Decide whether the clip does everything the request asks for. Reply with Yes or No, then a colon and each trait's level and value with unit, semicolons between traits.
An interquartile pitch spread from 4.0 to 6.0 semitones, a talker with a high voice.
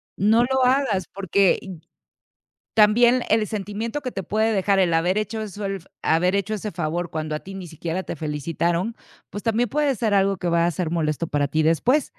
Yes: average, 4.6 semitones; high, 195 Hz